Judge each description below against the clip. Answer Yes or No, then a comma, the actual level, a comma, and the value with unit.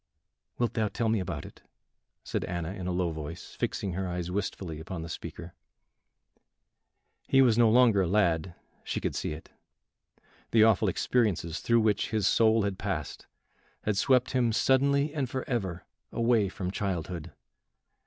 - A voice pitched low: Yes, low, 100 Hz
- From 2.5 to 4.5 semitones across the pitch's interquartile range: No, average, 4.9 semitones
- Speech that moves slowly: No, average, 155 wpm